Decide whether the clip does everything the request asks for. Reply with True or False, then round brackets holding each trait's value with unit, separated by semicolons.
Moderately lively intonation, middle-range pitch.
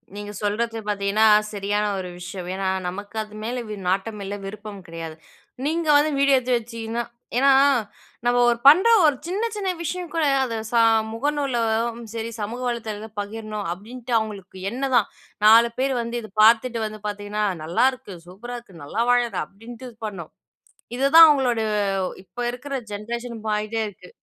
False (3.4 semitones; 225 Hz)